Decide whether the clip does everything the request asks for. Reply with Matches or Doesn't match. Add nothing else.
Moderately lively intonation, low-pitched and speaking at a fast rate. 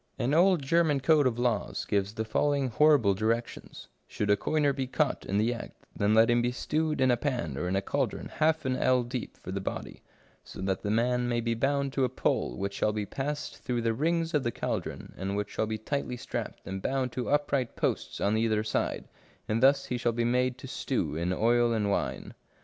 Matches